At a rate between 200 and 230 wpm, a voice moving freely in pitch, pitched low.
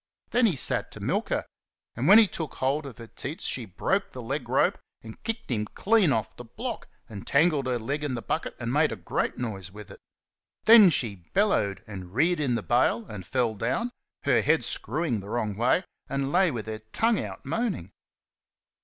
Yes: fast, 205 wpm; wide, 7.5 semitones; low, 125 Hz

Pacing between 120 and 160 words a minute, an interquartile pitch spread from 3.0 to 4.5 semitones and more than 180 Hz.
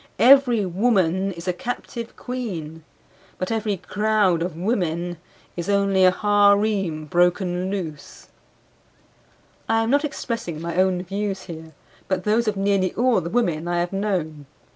Yes: average, 140 wpm; average, 3.5 semitones; high, 190 Hz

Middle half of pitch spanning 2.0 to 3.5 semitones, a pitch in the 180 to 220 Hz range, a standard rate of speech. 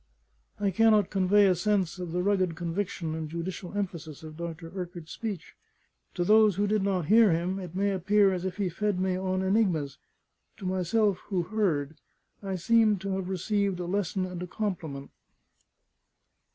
Yes: average, 2.8 semitones; medium, 185 Hz; average, 170 wpm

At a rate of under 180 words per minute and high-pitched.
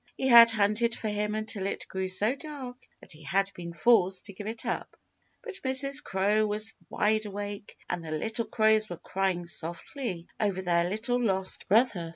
No: average, 185 wpm; high, 210 Hz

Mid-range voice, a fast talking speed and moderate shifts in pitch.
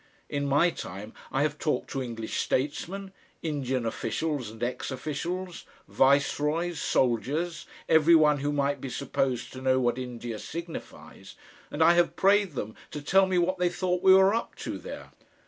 No: medium, 145 Hz; average, 165 wpm; average, 5.0 semitones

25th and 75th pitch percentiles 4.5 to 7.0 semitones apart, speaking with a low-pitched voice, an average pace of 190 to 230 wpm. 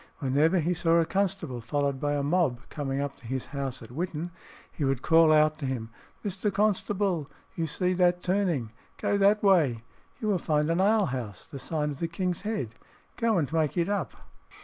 No: average, 4.9 semitones; medium, 160 Hz; average, 195 wpm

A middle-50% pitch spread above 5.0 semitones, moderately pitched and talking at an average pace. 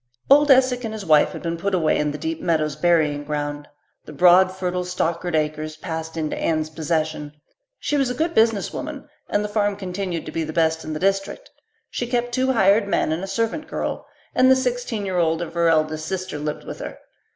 No: wide, 5.6 semitones; medium, 175 Hz; fast, 215 wpm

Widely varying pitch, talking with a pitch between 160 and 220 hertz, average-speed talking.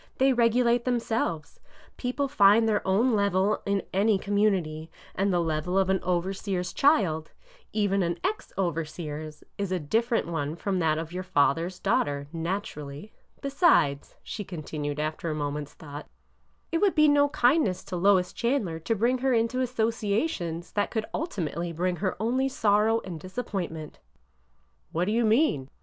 Yes: wide, 6.0 semitones; high, 190 Hz; average, 165 wpm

